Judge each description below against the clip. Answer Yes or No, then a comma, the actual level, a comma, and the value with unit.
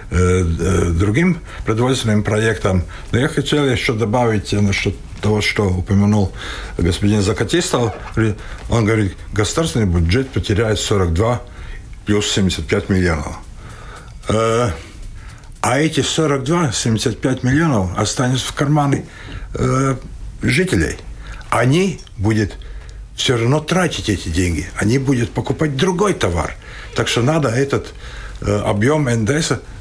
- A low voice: Yes, low, 110 Hz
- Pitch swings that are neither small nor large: Yes, average, 5.0 semitones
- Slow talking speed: Yes, slow, 100 wpm